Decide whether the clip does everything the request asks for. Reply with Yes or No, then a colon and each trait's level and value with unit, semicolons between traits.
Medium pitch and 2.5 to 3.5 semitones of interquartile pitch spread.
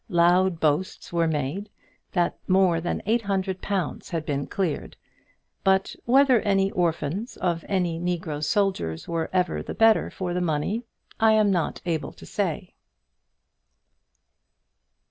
Yes: medium, 180 Hz; average, 3.1 semitones